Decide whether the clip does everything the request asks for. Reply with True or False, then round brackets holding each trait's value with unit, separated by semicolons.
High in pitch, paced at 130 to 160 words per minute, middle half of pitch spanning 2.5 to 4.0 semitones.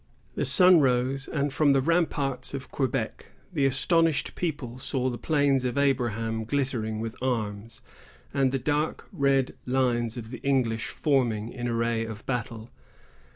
False (130 Hz; 150 wpm; 3.2 semitones)